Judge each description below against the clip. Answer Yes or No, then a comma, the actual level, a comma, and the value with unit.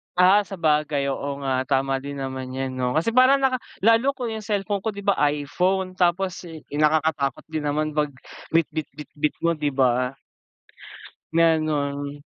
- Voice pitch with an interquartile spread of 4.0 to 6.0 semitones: Yes, average, 5.1 semitones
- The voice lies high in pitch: No, medium, 155 Hz